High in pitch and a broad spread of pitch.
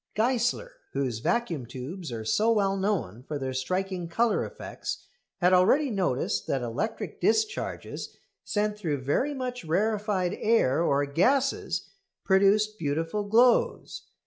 Yes: high, 195 Hz; wide, 7.5 semitones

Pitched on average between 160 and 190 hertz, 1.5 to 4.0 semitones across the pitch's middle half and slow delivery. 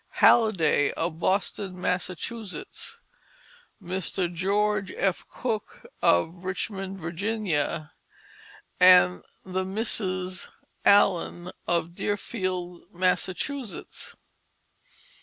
Yes: medium, 185 Hz; narrow, 2.6 semitones; slow, 70 wpm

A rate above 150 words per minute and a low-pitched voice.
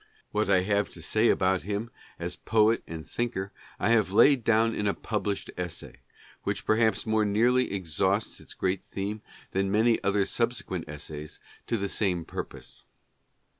Yes: average, 160 wpm; low, 100 Hz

